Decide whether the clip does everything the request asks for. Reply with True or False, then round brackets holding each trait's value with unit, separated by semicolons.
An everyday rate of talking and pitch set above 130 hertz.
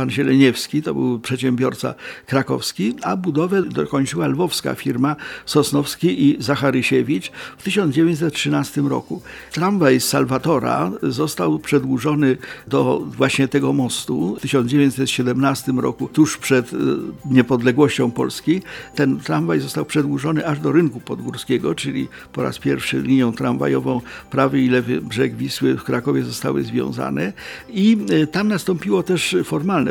True (120 wpm; 140 Hz)